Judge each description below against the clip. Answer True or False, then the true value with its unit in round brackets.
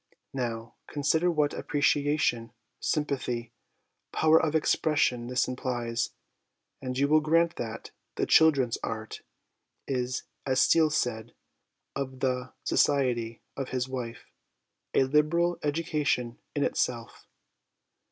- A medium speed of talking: False (120 wpm)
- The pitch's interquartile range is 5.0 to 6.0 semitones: False (3.8 semitones)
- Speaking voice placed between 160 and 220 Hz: False (130 Hz)